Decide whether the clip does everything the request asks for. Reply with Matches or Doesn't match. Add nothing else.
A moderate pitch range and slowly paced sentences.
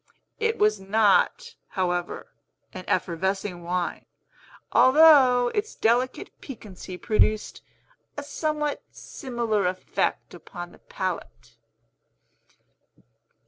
Doesn't match